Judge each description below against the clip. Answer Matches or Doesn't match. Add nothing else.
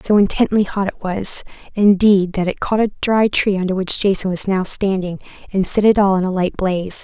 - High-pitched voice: Matches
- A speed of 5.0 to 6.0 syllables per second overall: Matches